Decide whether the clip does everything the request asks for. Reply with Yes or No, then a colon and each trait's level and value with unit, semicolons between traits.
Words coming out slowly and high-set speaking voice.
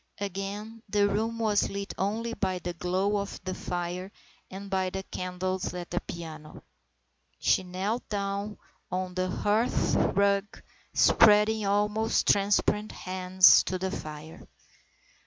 Yes: slow, 130 wpm; high, 195 Hz